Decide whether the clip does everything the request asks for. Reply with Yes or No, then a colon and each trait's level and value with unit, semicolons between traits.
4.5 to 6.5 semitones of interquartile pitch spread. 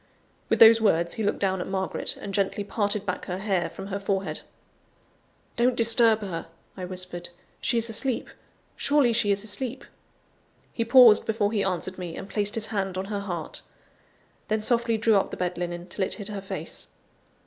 No: average, 3.1 semitones